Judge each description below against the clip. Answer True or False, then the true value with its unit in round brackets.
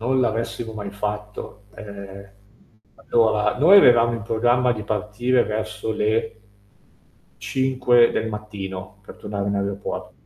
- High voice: False (110 Hz)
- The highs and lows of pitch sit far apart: False (2.7 semitones)